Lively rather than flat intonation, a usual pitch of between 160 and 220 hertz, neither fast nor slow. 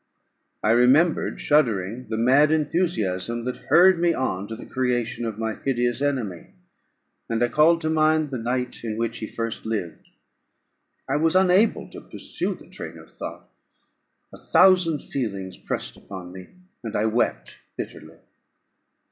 No: wide, 5.7 semitones; low, 120 Hz; average, 150 wpm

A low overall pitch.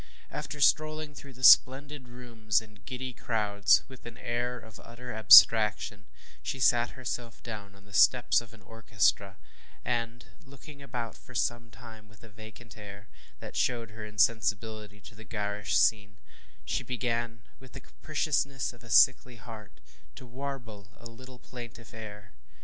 Yes: low, 115 Hz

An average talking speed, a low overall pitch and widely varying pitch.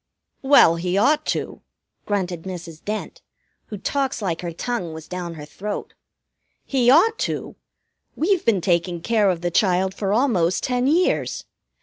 No: average, 150 wpm; high, 195 Hz; wide, 6.3 semitones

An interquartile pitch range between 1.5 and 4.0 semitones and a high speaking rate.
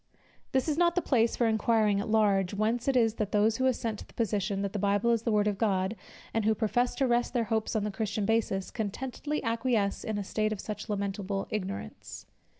Yes: narrow, 2.5 semitones; fast, 225 wpm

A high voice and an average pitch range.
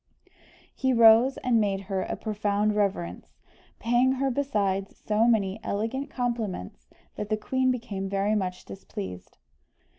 Yes: high, 210 Hz; average, 3.6 semitones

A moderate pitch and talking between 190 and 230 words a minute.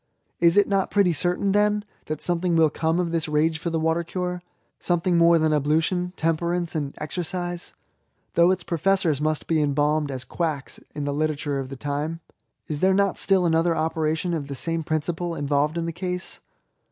Yes: medium, 165 Hz; average, 200 wpm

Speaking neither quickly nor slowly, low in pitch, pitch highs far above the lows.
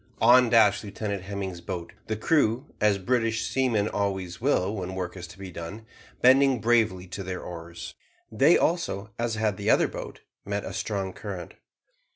No: average, 170 wpm; low, 100 Hz; average, 3.4 semitones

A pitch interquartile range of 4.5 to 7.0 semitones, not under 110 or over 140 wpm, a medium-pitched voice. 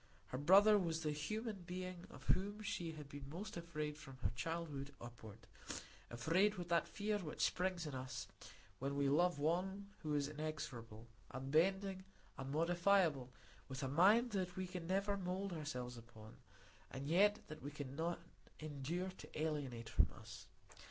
No: average, 5.0 semitones; average, 155 wpm; medium, 160 Hz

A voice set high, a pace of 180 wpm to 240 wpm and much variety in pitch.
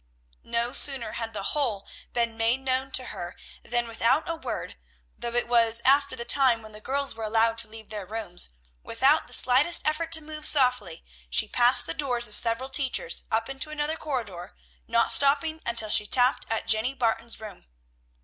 No: high, 240 Hz; average, 185 wpm; average, 3.7 semitones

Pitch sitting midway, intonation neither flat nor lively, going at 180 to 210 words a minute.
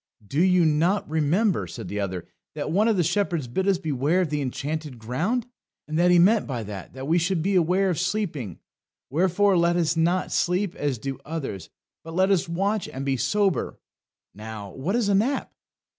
No: medium, 165 Hz; wide, 5.7 semitones; average, 190 wpm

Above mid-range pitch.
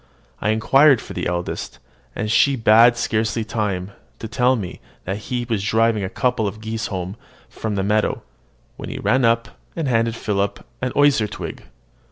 No: low, 110 Hz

